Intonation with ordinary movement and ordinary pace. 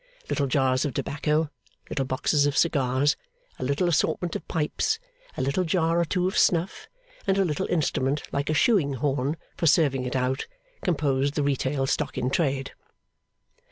Yes: average, 3.5 semitones; average, 165 wpm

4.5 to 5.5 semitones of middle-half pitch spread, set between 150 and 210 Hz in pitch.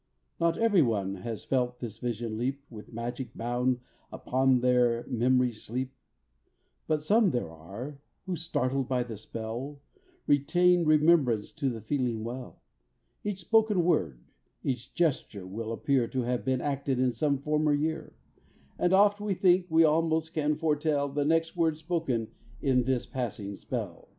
No: average, 5.0 semitones; low, 130 Hz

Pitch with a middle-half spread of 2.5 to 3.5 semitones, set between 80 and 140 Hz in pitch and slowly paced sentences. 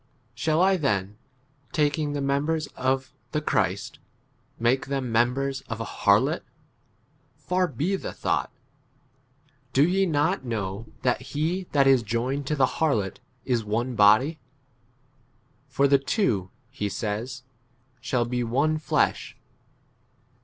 No: average, 4.4 semitones; low, 135 Hz; slow, 130 wpm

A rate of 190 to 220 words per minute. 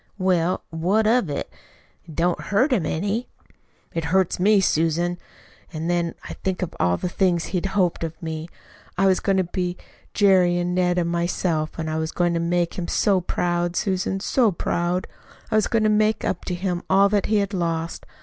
Yes: average, 195 wpm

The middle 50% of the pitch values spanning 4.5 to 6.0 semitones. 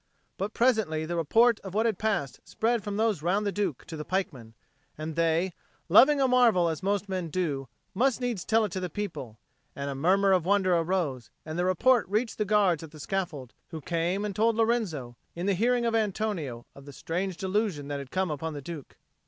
Yes: average, 5.1 semitones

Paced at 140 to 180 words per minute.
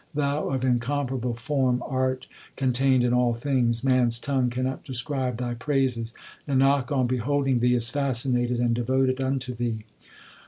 Yes: average, 150 wpm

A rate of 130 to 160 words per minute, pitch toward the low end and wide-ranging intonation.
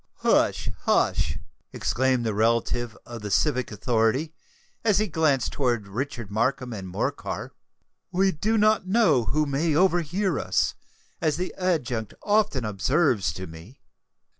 Yes: slow, 135 wpm; low, 130 Hz; wide, 7.3 semitones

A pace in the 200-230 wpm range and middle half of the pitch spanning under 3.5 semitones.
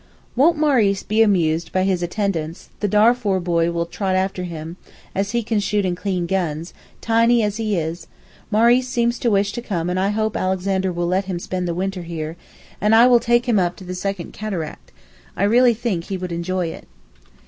No: fast, 205 wpm; average, 3.8 semitones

